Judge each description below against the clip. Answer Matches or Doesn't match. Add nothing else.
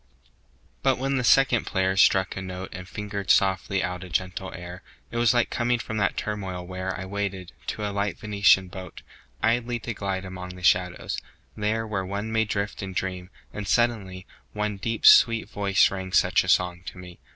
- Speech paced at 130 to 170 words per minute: Doesn't match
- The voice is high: Doesn't match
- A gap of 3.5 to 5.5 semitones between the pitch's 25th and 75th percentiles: Doesn't match